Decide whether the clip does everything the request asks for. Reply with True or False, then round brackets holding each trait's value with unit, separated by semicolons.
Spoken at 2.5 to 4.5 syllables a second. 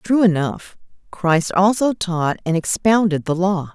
True (3.9 syllables/s)